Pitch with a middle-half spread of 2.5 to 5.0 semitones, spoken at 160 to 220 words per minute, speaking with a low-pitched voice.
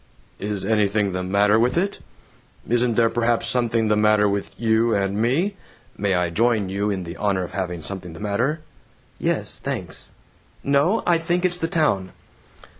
Yes: average, 3.7 semitones; average, 170 wpm; low, 105 Hz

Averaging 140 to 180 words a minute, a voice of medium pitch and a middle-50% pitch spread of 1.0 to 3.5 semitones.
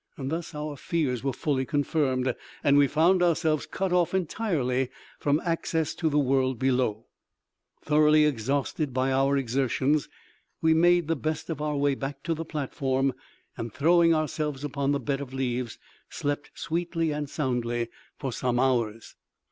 Yes: average, 155 wpm; medium, 145 Hz; average, 3.1 semitones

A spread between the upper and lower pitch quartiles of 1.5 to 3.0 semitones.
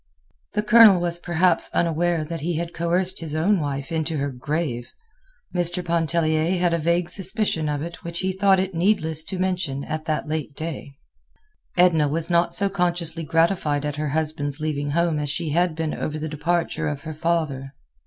Yes: narrow, 2.4 semitones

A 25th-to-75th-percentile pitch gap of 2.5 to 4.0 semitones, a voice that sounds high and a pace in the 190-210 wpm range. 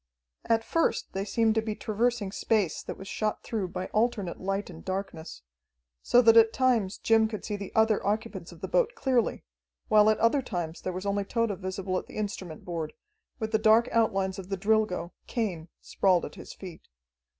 Yes: average, 3.1 semitones; high, 210 Hz; average, 195 wpm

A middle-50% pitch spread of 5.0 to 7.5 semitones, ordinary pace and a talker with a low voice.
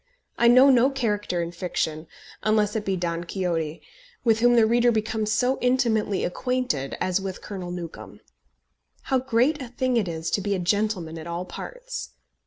No: wide, 5.6 semitones; average, 175 wpm; high, 210 Hz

